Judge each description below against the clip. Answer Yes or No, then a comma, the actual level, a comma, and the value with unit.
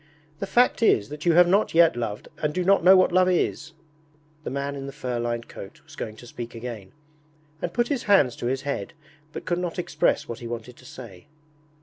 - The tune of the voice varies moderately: No, wide, 6.9 semitones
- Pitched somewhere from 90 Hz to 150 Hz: Yes, medium, 140 Hz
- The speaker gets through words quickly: Yes, fast, 225 wpm